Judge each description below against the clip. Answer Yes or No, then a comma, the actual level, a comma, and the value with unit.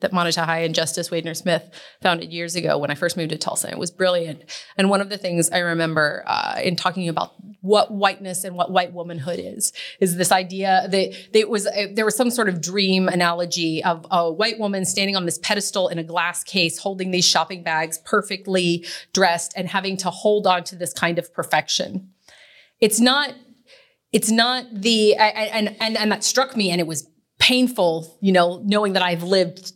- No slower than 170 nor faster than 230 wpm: Yes, fast, 205 wpm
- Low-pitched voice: No, medium, 185 Hz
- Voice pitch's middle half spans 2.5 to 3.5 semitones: Yes, average, 3.1 semitones